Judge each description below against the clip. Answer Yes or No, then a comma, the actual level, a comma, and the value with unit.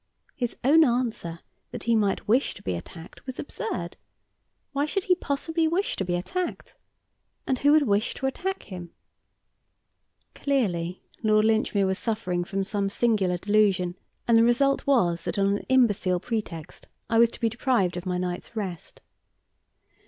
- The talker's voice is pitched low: No, high, 215 Hz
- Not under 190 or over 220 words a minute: No, average, 160 wpm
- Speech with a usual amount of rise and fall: No, wide, 6.2 semitones